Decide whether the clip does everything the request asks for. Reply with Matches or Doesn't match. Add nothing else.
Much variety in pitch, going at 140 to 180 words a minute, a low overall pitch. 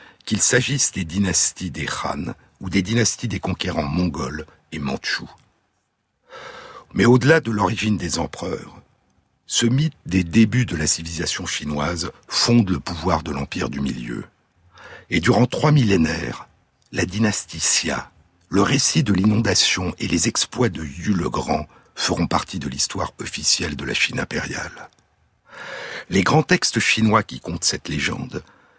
Matches